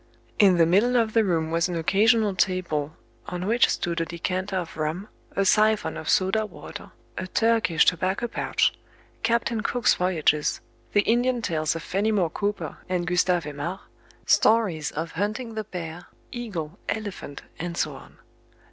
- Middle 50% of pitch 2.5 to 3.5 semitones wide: No, average, 4.4 semitones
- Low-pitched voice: No, medium, 185 Hz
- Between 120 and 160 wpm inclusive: Yes, average, 155 wpm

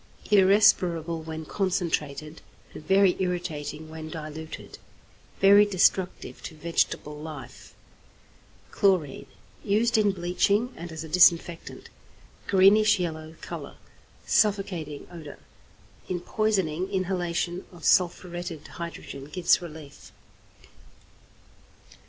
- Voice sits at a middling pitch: Yes, medium, 175 Hz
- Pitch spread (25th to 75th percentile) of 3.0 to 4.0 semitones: Yes, average, 3.4 semitones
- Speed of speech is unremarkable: No, slow, 95 wpm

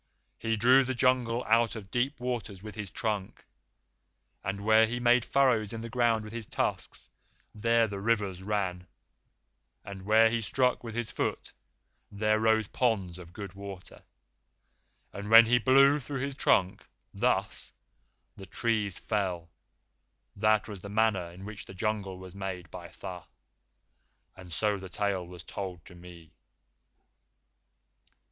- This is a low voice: Yes, low, 105 Hz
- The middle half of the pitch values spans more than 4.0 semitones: No, average, 3.4 semitones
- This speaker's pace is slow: No, average, 150 wpm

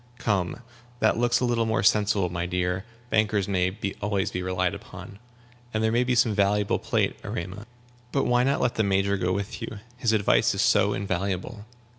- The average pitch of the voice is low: Yes, low, 100 Hz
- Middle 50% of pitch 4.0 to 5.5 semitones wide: No, average, 3.3 semitones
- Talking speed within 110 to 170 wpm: No, average, 185 wpm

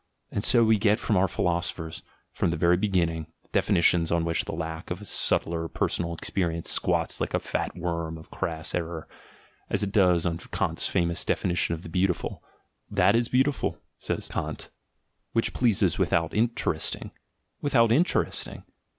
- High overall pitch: No, very low, 85 Hz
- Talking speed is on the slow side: No, average, 160 wpm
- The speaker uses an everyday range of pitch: Yes, average, 3.8 semitones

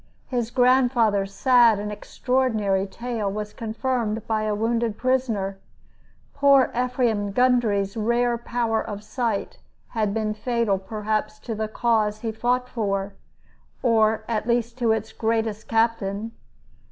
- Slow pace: Yes, slow, 130 wpm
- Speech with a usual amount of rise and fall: No, narrow, 2.3 semitones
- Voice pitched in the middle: No, high, 225 Hz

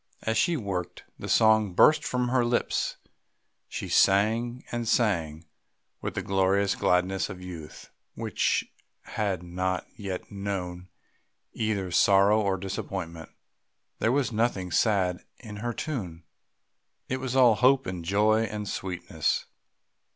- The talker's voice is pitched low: Yes, low, 100 Hz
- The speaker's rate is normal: No, slow, 130 wpm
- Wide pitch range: No, average, 3.8 semitones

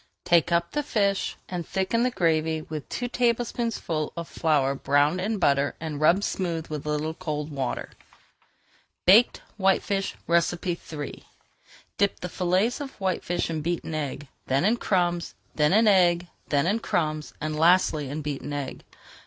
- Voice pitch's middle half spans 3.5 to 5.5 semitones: Yes, average, 4.1 semitones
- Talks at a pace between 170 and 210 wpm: No, average, 155 wpm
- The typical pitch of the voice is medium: Yes, medium, 170 Hz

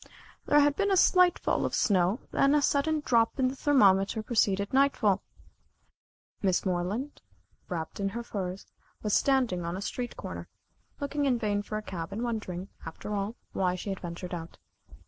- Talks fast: No, average, 175 wpm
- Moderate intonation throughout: No, wide, 6.1 semitones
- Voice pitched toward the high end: Yes, high, 210 Hz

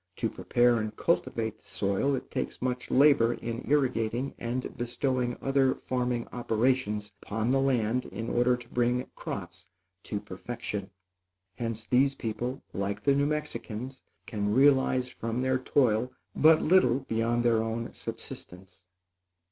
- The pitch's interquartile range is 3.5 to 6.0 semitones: No, average, 2.8 semitones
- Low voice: Yes, low, 120 Hz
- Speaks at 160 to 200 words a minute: No, average, 140 wpm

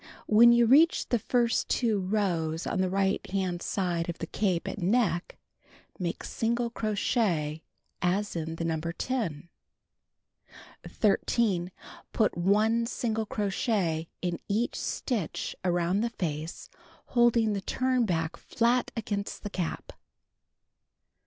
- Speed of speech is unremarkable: No, slow, 125 wpm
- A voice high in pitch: Yes, high, 200 Hz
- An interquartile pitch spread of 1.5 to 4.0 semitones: No, average, 5.1 semitones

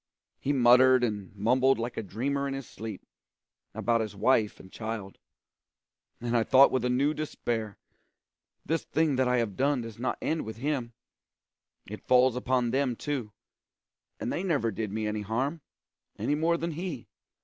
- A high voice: No, low, 125 Hz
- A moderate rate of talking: Yes, average, 170 wpm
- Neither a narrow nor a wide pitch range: Yes, average, 3.9 semitones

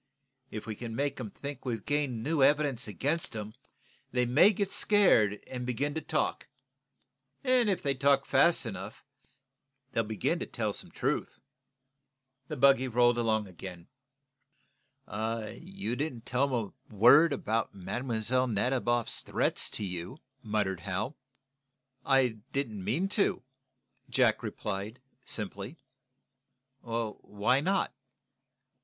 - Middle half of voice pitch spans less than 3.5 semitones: No, average, 4.7 semitones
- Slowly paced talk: Yes, slow, 125 wpm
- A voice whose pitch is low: Yes, low, 120 Hz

